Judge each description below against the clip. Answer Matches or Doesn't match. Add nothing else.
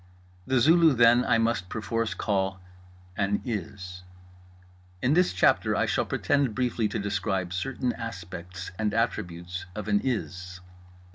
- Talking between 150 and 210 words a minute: Doesn't match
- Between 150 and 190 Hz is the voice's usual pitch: Doesn't match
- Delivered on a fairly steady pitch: Doesn't match